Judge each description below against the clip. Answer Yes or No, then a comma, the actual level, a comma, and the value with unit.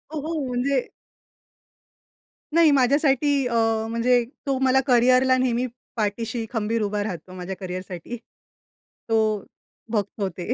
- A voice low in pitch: No, high, 240 Hz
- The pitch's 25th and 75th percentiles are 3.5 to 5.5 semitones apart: Yes, average, 4.0 semitones